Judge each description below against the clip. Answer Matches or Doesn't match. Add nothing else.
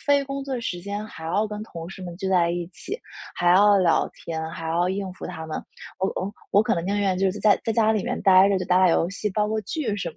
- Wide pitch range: Doesn't match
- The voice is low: Doesn't match